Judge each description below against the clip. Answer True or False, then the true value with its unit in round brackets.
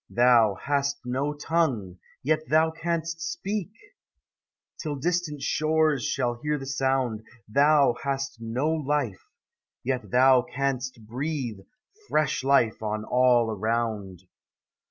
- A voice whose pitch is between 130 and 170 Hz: True (135 Hz)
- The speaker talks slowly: True (115 wpm)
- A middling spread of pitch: True (4.2 semitones)